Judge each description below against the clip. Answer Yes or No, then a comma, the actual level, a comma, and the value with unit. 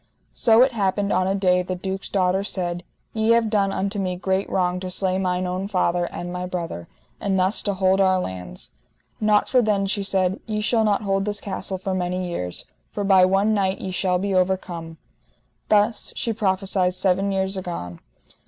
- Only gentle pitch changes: Yes, narrow, 1.7 semitones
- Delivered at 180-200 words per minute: Yes, average, 190 wpm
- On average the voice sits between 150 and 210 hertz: Yes, high, 190 Hz